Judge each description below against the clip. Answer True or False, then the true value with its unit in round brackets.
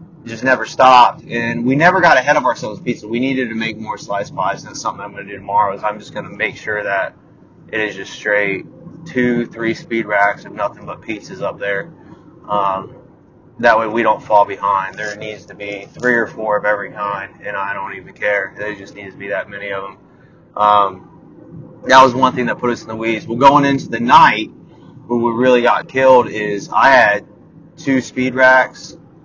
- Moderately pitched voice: False (115 Hz)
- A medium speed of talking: False (215 wpm)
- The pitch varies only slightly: False (4.0 semitones)